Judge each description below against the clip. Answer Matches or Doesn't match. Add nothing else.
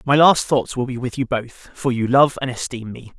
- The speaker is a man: Matches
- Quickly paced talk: Matches